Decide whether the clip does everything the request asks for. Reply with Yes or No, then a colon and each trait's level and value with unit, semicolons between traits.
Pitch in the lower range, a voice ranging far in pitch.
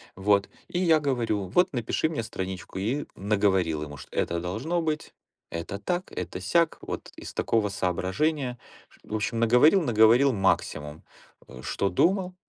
Yes: low, 110 Hz; wide, 8.1 semitones